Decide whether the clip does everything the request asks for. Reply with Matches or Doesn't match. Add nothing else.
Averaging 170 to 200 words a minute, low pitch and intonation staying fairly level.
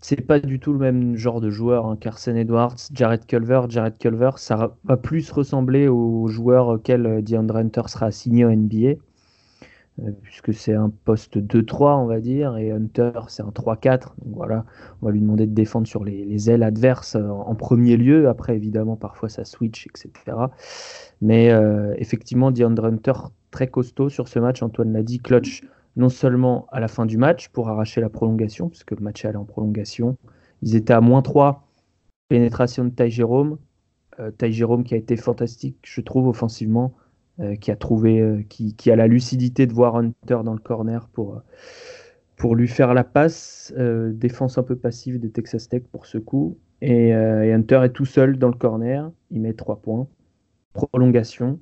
Matches